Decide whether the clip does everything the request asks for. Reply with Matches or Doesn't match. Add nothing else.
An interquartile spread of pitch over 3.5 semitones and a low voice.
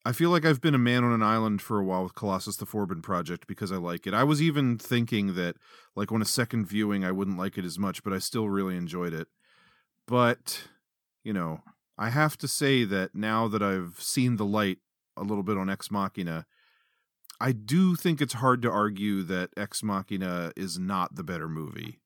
Matches